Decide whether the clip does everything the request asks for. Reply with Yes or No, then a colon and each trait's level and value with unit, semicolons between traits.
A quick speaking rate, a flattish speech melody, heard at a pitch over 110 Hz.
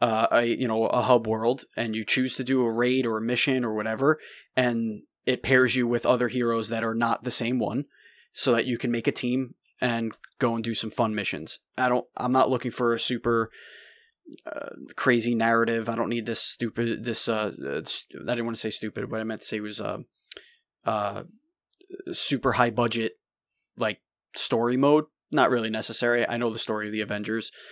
Yes: fast, 210 wpm; narrow, 2.1 semitones; low, 120 Hz